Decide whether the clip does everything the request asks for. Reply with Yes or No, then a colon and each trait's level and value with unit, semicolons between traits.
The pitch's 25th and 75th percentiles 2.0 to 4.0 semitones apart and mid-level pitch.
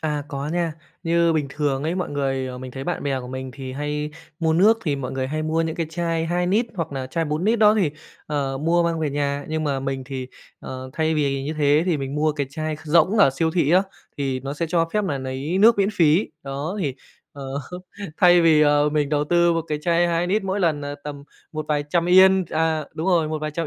Yes: average, 3.3 semitones; medium, 155 Hz